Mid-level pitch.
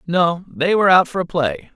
Yes: medium, 170 Hz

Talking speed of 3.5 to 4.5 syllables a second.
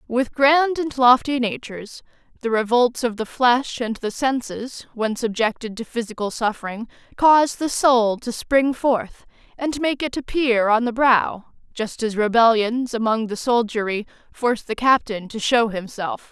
Yes: 4.4 syllables/s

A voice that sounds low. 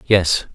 Yes: very low, 90 Hz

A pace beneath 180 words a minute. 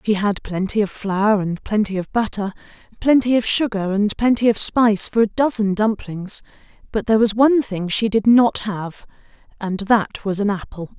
No: average, 185 wpm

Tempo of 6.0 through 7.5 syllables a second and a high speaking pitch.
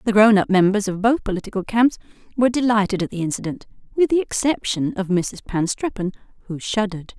Yes: 6.1 syllables/s; high, 210 Hz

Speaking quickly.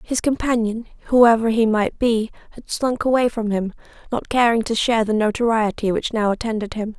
No: average, 180 wpm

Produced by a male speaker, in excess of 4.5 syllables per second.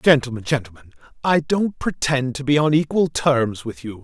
Yes: male; 4.9 syllables/s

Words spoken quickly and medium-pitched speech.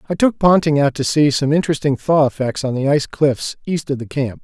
Yes: fast, 245 wpm; medium, 145 Hz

